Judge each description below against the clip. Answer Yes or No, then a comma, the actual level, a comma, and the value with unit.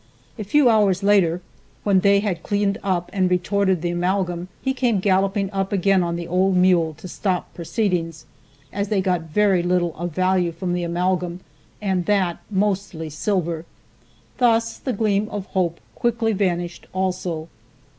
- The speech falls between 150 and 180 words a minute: Yes, average, 155 wpm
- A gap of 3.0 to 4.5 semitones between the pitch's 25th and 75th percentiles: No, narrow, 2.6 semitones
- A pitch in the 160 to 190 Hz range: Yes, medium, 185 Hz